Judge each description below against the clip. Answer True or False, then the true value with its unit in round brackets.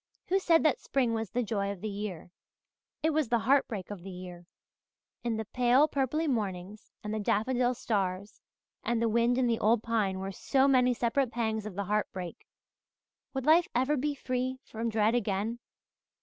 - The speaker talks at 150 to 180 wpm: False (190 wpm)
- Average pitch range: True (3.9 semitones)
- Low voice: False (230 Hz)